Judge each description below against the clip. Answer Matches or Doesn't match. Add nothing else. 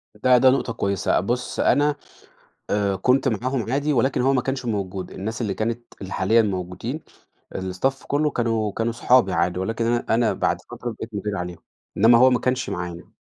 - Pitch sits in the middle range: Doesn't match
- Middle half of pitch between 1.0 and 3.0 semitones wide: Doesn't match